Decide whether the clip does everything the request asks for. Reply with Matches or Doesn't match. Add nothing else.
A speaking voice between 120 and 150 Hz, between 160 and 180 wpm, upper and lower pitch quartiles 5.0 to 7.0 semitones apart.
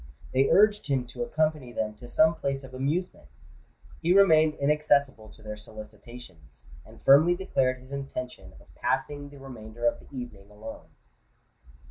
Doesn't match